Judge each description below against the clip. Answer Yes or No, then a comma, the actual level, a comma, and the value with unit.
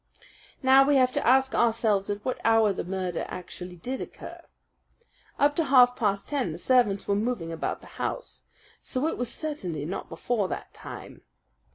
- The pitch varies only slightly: No, average, 5.1 semitones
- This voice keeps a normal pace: Yes, average, 175 wpm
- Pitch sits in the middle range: No, high, 230 Hz